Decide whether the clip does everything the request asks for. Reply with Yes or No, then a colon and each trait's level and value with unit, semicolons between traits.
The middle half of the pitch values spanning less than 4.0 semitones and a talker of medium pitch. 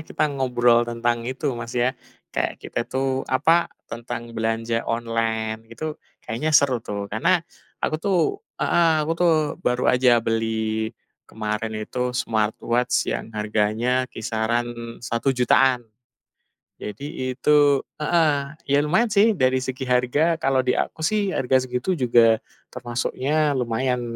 No: average, 2.8 semitones; low, 125 Hz